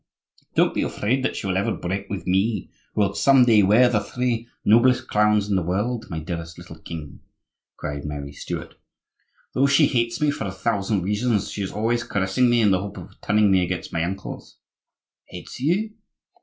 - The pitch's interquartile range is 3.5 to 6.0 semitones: Yes, average, 4.2 semitones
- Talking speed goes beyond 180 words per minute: Yes, average, 195 wpm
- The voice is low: Yes, low, 105 Hz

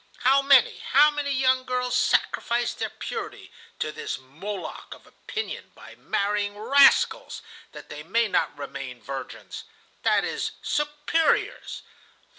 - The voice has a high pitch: Yes, high, 245 Hz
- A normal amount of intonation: No, wide, 9.0 semitones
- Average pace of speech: No, slow, 120 wpm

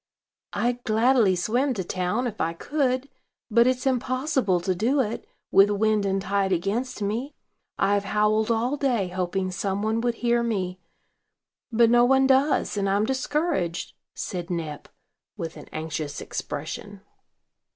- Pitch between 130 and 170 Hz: No, high, 215 Hz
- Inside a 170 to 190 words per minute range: No, average, 145 wpm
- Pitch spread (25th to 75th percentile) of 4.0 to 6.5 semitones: Yes, average, 4.7 semitones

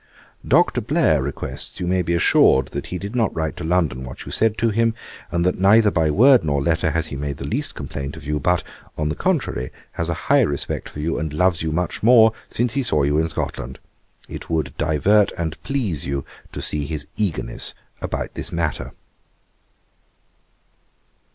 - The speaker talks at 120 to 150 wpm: No, average, 195 wpm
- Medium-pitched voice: No, very low, 80 Hz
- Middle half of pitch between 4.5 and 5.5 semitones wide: Yes, average, 5.2 semitones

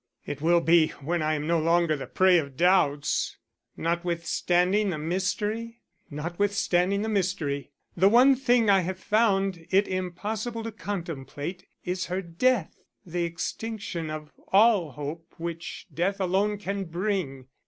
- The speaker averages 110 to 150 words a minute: Yes, average, 140 wpm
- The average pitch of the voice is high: No, medium, 180 Hz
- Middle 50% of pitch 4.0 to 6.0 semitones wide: No, average, 3.5 semitones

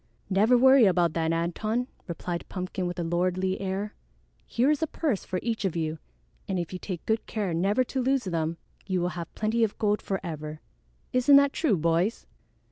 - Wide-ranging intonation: No, average, 5.0 semitones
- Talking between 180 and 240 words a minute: Yes, average, 190 wpm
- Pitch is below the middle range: No, high, 190 Hz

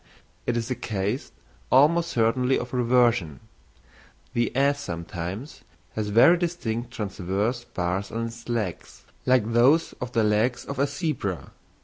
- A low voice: Yes, low, 120 Hz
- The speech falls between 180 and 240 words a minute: No, slow, 135 wpm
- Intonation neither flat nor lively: Yes, average, 3.7 semitones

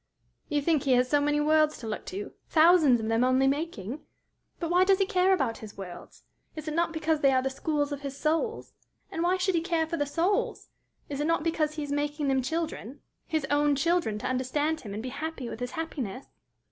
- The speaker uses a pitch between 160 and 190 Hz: No, very high, 295 Hz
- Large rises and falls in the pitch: No, average, 3.9 semitones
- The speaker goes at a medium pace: No, fast, 225 wpm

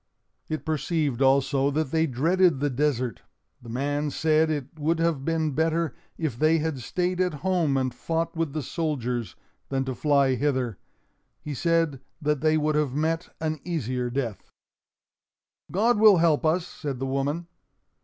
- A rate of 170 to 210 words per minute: No, average, 160 wpm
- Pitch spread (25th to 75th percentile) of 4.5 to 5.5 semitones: No, average, 3.3 semitones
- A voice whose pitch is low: No, medium, 150 Hz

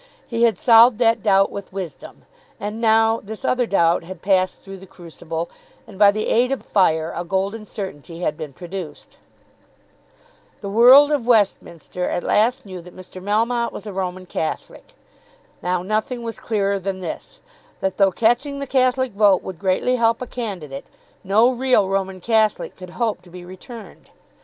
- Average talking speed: Yes, average, 170 wpm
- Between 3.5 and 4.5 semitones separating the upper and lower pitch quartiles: Yes, average, 3.9 semitones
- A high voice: Yes, high, 200 Hz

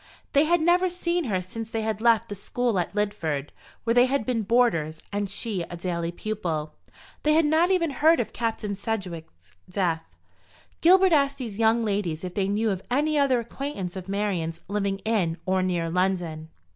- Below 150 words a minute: No, average, 185 wpm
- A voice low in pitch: No, high, 210 Hz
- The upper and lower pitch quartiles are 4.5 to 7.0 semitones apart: Yes, wide, 5.6 semitones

